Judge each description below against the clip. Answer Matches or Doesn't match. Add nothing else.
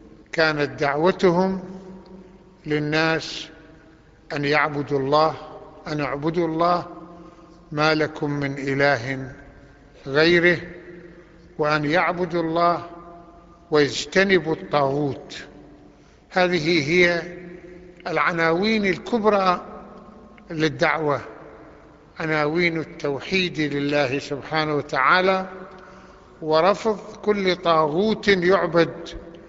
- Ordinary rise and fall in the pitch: Matches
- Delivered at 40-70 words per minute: Matches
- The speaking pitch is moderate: Matches